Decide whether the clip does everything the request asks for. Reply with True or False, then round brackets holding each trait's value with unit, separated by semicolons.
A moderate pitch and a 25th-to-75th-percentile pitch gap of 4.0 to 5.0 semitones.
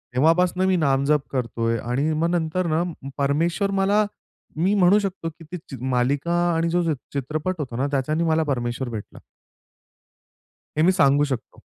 True (155 Hz; 4.5 semitones)